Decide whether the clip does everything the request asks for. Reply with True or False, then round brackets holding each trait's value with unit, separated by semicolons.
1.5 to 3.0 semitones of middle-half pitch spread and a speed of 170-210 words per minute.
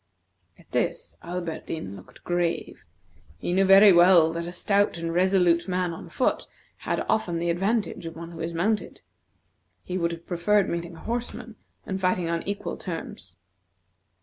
False (2.4 semitones; 160 wpm)